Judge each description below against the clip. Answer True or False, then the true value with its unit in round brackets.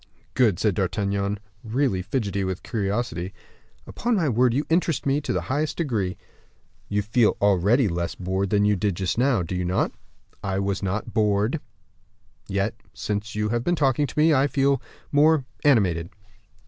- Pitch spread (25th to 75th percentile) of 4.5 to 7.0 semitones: True (5.6 semitones)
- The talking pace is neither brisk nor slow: True (165 wpm)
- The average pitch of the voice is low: True (105 Hz)